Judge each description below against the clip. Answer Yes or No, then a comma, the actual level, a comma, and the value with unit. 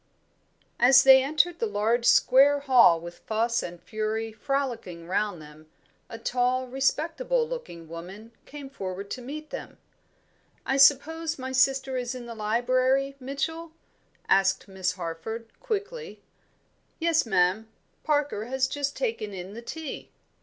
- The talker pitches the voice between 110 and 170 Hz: No, very high, 255 Hz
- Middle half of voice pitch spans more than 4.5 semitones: Yes, average, 5.2 semitones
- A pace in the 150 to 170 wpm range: No, slow, 135 wpm